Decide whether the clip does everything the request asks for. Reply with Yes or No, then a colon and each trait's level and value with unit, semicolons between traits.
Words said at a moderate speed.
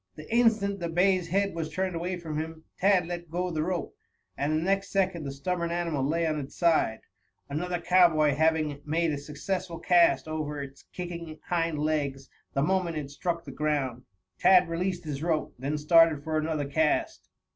Yes: average, 180 wpm